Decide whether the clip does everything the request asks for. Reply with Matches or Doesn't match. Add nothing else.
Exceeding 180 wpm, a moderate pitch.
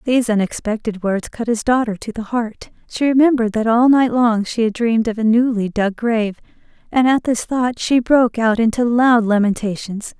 Doesn't match